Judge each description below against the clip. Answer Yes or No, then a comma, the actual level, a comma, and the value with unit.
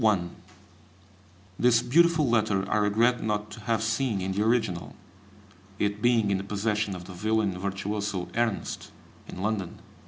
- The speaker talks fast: No, average, 155 wpm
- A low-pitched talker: Yes, low, 105 Hz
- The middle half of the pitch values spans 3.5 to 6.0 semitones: No, narrow, 2.6 semitones